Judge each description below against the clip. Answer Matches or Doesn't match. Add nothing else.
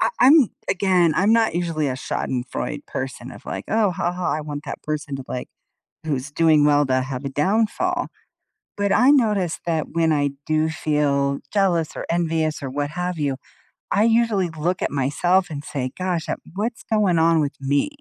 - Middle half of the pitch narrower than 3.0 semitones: Doesn't match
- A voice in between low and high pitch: Matches